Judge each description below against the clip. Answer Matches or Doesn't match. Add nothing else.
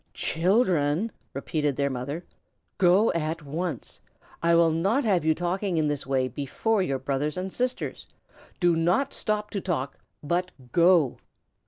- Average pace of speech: Matches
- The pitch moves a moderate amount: Matches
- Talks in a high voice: Doesn't match